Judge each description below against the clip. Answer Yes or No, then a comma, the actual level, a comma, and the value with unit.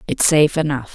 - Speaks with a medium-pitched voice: Yes, medium, 150 Hz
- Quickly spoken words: No, average, 190 wpm